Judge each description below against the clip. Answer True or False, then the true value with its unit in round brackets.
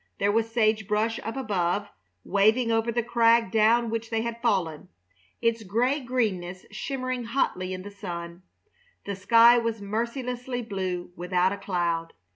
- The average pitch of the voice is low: False (220 Hz)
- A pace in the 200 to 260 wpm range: False (150 wpm)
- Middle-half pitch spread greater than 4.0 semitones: False (3.7 semitones)